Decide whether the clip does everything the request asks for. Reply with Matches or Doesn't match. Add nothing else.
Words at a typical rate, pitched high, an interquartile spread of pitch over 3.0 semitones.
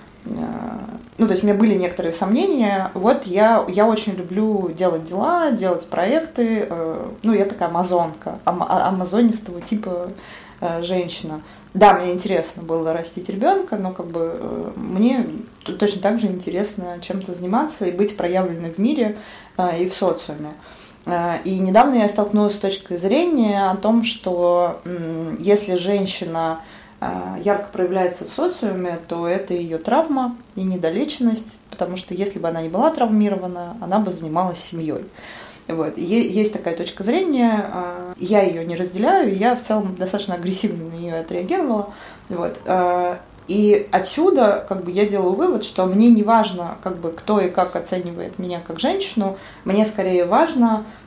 Matches